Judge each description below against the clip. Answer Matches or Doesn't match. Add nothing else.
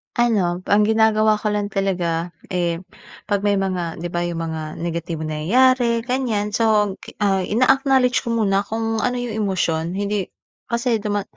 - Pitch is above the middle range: Matches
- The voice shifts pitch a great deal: Doesn't match